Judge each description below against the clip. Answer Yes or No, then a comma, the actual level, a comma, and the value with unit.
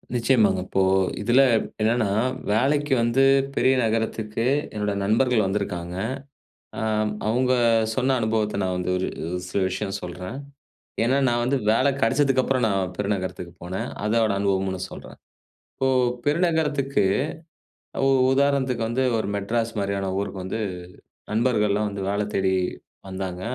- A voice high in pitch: No, low, 110 Hz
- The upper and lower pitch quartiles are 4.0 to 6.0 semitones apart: Yes, average, 4.5 semitones